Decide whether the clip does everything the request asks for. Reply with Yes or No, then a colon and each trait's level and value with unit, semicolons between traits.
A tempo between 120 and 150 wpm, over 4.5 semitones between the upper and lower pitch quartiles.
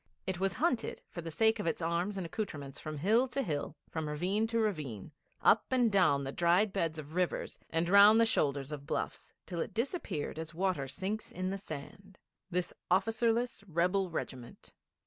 No: average, 185 wpm; average, 5.2 semitones